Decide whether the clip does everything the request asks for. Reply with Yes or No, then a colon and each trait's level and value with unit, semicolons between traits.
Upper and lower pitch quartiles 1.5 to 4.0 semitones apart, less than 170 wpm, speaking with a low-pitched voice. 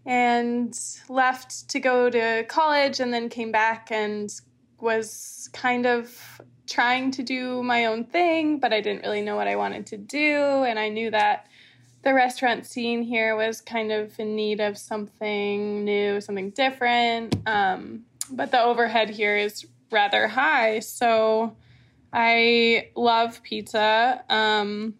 No: average, 2.7 semitones; average, 145 wpm; high, 225 Hz